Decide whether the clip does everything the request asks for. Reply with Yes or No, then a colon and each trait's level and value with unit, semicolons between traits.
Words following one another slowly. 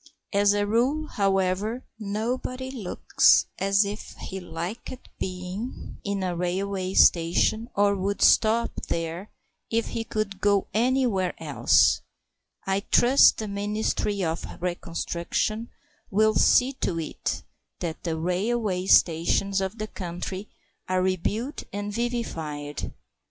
Yes: slow, 120 wpm